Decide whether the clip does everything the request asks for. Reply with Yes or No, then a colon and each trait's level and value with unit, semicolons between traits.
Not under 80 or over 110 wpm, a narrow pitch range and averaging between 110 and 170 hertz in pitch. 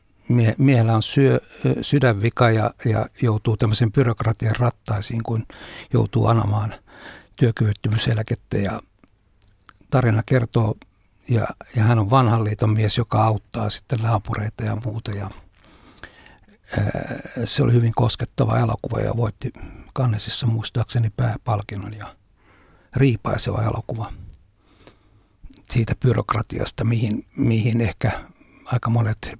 Yes: average, 105 wpm; narrow, 2.1 semitones; low, 115 Hz